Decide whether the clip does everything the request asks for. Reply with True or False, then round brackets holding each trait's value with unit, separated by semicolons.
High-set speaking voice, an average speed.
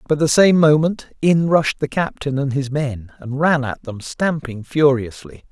False (140 Hz; 185 wpm)